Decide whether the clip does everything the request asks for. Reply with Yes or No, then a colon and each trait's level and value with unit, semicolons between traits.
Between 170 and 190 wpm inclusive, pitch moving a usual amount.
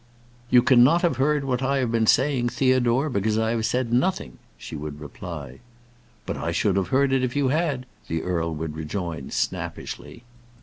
No: average, 180 wpm; wide, 7.7 semitones